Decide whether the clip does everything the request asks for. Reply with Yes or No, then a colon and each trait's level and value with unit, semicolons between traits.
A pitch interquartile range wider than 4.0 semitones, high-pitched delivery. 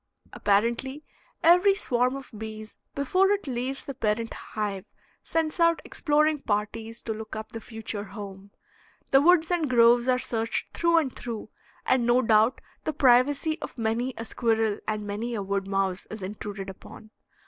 Yes: average, 4.5 semitones; high, 235 Hz